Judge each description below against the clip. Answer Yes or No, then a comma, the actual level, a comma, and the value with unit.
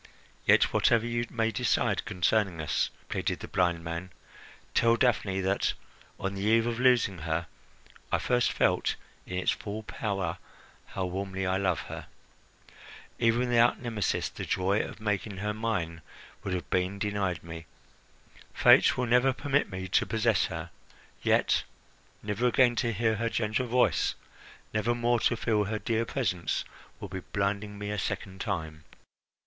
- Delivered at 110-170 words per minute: Yes, average, 155 wpm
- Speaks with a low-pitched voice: Yes, low, 105 Hz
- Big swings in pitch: No, average, 3.8 semitones